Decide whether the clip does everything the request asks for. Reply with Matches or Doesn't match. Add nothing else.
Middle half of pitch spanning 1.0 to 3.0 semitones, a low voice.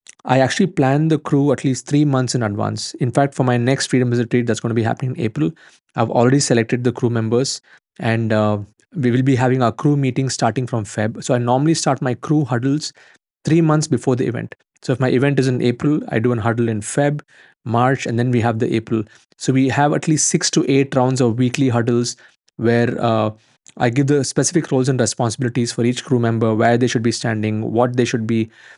Matches